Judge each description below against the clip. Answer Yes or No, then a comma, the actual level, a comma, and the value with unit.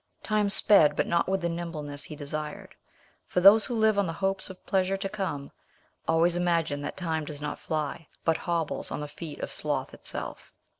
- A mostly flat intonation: No, average, 4.2 semitones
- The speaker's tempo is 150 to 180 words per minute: No, average, 195 wpm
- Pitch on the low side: No, medium, 170 Hz